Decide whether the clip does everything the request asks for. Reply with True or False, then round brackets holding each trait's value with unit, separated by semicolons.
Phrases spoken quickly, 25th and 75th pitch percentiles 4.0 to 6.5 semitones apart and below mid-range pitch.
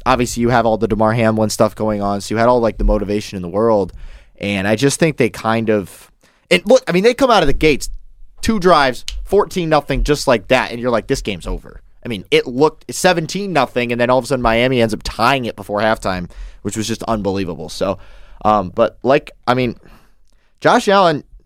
True (225 wpm; 4.7 semitones; 115 Hz)